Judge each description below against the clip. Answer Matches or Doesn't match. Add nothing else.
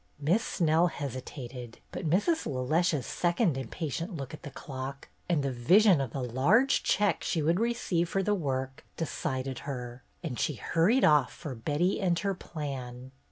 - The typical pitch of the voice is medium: Matches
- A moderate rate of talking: Matches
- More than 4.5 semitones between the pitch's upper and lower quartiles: Matches